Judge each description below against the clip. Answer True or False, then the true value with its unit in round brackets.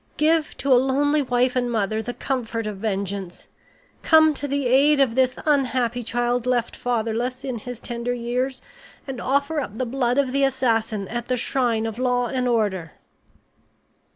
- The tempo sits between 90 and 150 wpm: False (170 wpm)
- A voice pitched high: True (245 Hz)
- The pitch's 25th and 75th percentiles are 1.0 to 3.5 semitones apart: True (2.6 semitones)